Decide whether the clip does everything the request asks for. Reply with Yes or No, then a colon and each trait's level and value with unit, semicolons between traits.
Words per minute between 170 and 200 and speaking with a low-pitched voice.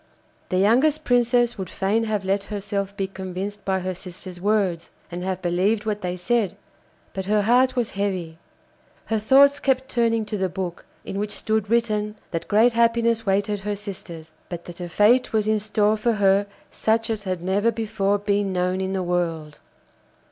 No: average, 180 wpm; high, 205 Hz